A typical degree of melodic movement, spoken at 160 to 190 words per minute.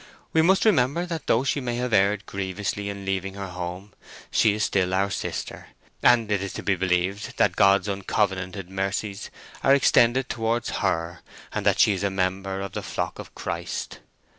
Yes: average, 3.0 semitones; average, 185 wpm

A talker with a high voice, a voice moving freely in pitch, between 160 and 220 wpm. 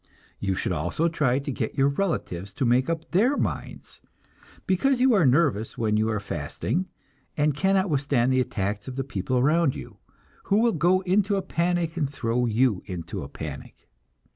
No: medium, 140 Hz; wide, 7.5 semitones; average, 180 wpm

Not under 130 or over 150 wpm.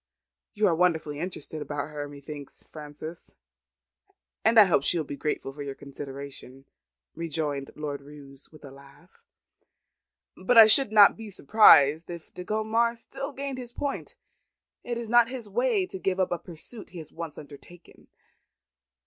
No: average, 160 wpm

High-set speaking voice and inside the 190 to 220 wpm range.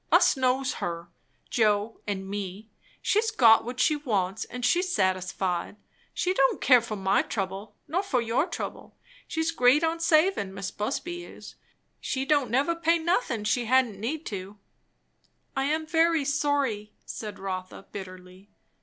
No: high, 245 Hz; average, 150 wpm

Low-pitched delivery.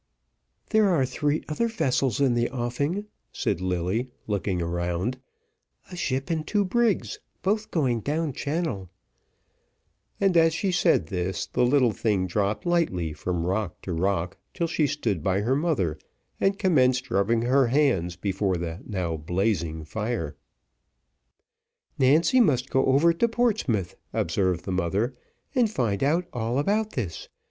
Yes: low, 120 Hz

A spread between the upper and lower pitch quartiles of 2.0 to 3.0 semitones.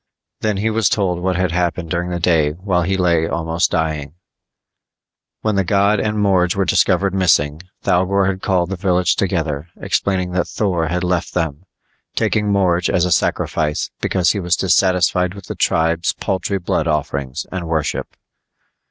Yes: narrow, 2.6 semitones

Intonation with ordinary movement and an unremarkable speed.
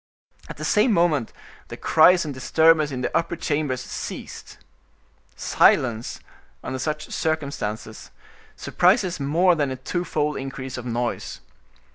No: average, 4.0 semitones; slow, 125 wpm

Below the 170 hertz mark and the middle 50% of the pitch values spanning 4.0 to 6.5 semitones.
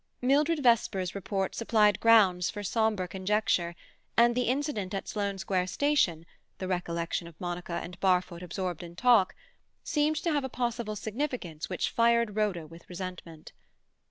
No: high, 200 Hz; average, 4.7 semitones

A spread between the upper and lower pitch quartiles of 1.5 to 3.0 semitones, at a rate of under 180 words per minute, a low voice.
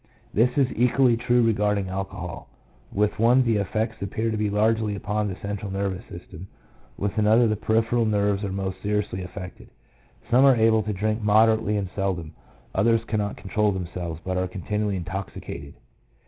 Yes: narrow, 2.5 semitones; average, 160 wpm; low, 105 Hz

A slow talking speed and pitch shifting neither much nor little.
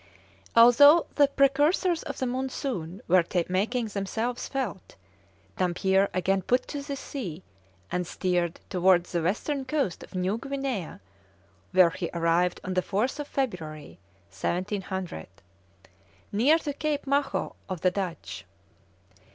No: slow, 120 wpm; wide, 7.1 semitones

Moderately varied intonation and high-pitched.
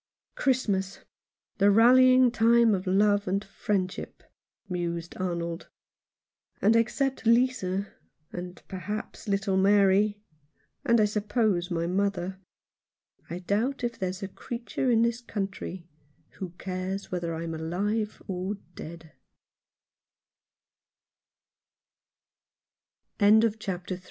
Yes: average, 3.6 semitones; high, 200 Hz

